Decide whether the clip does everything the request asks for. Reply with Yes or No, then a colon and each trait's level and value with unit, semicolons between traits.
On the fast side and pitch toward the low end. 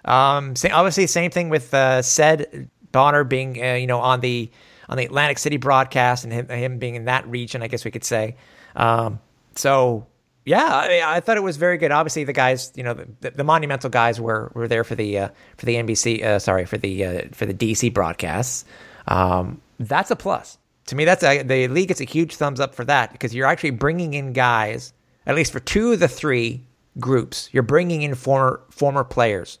Yes: fast, 220 wpm; low, 130 Hz